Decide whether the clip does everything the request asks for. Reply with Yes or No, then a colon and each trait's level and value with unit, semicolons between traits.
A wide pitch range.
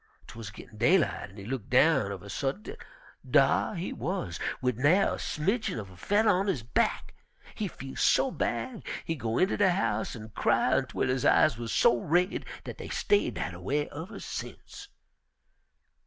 Yes: wide, 8.8 semitones